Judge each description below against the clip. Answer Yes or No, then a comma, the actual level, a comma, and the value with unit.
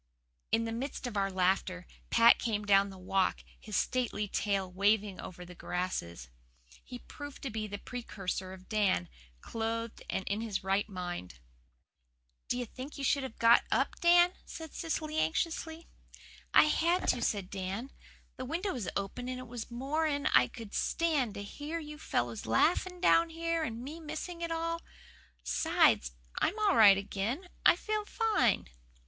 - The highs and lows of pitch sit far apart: Yes, wide, 8.0 semitones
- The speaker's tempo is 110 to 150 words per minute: No, average, 165 wpm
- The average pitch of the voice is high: Yes, high, 230 Hz